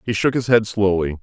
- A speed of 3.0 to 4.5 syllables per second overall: No, 5.6 syllables/s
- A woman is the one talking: No, male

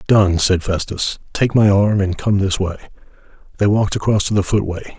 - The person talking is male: Yes, male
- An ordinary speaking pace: Yes, average, 195 wpm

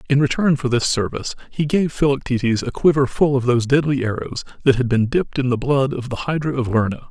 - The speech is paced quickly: Yes, fast, 230 wpm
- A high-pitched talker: No, low, 130 Hz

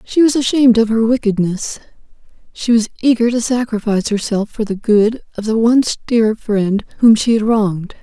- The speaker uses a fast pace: No, average, 180 wpm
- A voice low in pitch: No, high, 225 Hz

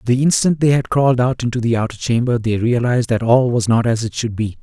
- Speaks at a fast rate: Yes, fast, 260 wpm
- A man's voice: Yes, male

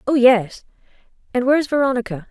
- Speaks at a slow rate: Yes, slow, 130 wpm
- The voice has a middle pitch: No, very high, 250 Hz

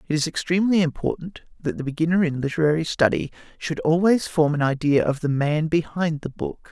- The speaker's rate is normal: Yes, average, 190 wpm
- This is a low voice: No, medium, 160 Hz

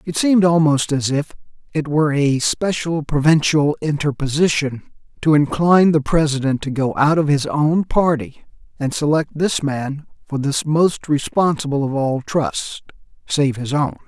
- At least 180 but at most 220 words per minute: No, average, 155 wpm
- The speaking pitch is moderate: Yes, medium, 150 Hz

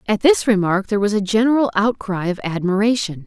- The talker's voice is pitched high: Yes, high, 210 Hz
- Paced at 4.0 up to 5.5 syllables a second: No, 5.9 syllables/s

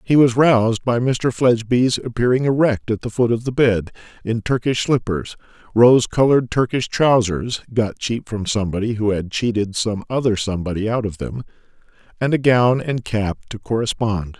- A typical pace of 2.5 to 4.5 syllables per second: Yes, 3.6 syllables/s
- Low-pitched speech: Yes, low, 115 Hz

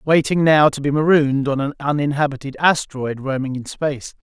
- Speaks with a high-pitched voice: No, medium, 145 Hz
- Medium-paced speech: Yes, average, 165 wpm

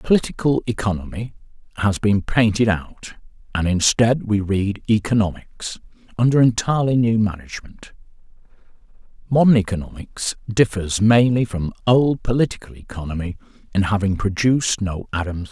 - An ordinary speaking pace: No, slow, 110 wpm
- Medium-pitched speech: No, low, 105 Hz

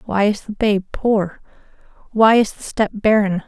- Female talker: Yes, female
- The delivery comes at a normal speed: Yes, average, 175 wpm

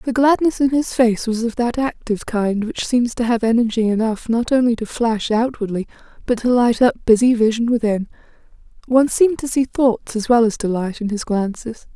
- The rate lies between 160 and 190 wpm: No, average, 200 wpm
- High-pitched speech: Yes, high, 235 Hz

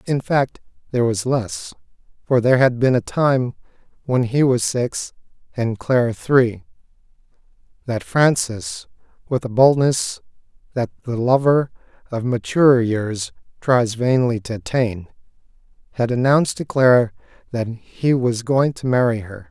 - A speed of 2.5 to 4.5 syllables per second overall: Yes, 4.3 syllables/s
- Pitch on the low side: Yes, low, 125 Hz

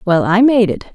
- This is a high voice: Yes, high, 210 Hz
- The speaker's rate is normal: No, fast, 255 wpm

